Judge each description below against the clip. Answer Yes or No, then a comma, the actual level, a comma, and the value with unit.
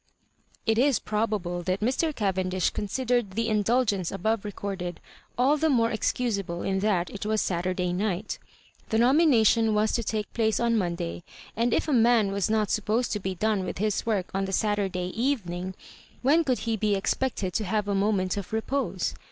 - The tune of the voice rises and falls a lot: No, average, 3.4 semitones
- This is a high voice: Yes, high, 210 Hz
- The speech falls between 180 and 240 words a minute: Yes, average, 190 wpm